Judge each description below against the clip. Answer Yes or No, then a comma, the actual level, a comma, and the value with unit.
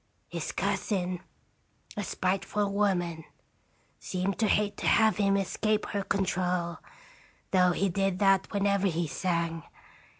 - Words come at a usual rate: No, slow, 125 wpm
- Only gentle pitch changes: Yes, narrow, 2.2 semitones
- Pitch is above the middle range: Yes, high, 195 Hz